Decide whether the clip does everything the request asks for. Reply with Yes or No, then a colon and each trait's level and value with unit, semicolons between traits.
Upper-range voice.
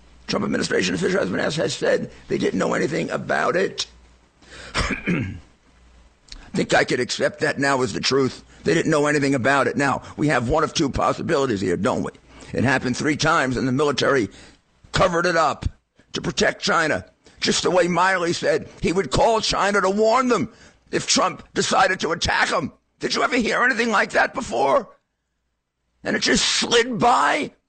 No: medium, 140 Hz